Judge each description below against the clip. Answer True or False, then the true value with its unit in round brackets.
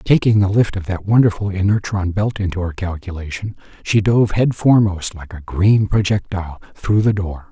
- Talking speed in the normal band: True (170 wpm)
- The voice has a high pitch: False (100 Hz)